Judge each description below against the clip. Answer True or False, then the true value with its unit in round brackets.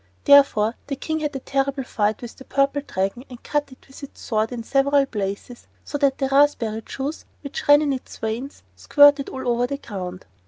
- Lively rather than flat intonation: False (3.7 semitones)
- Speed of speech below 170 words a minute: False (200 wpm)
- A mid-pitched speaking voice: False (270 Hz)